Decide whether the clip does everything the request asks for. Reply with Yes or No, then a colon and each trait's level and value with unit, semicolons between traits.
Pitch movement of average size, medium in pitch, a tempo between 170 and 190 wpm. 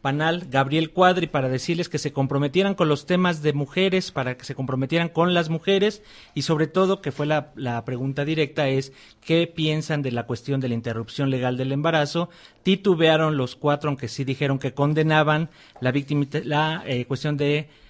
Yes: average, 3.3 semitones; medium, 150 Hz; average, 180 wpm